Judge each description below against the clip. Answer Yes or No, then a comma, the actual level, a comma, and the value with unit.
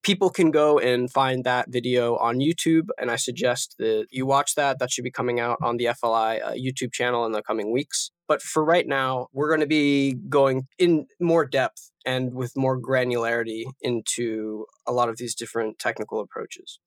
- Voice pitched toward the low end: Yes, low, 130 Hz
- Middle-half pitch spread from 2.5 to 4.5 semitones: Yes, average, 3.6 semitones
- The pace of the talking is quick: No, average, 195 wpm